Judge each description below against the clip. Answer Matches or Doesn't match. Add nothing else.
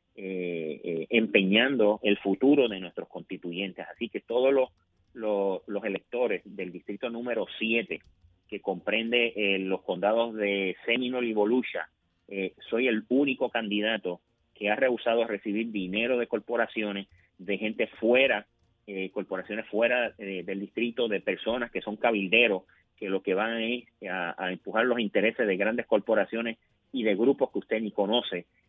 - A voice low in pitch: Matches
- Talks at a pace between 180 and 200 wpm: Doesn't match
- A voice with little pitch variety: Doesn't match